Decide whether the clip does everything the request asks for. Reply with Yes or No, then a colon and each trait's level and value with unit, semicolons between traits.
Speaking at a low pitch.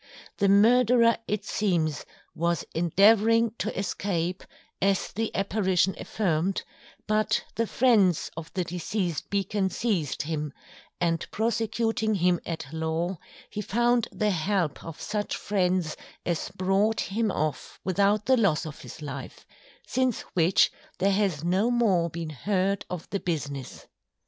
No: high, 190 Hz